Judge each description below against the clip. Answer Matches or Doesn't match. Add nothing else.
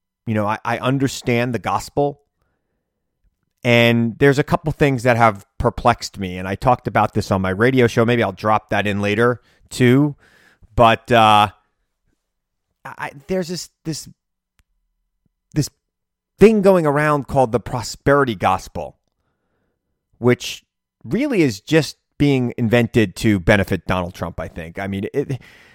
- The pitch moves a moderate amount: Doesn't match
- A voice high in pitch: Doesn't match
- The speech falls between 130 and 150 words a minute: Matches